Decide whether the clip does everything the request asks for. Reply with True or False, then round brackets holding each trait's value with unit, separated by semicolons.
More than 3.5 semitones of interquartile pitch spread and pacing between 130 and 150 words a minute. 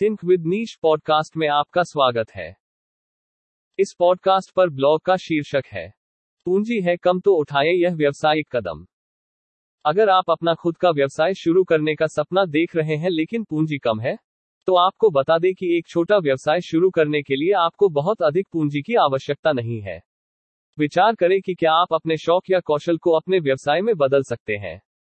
False (4.1 semitones; 180 wpm)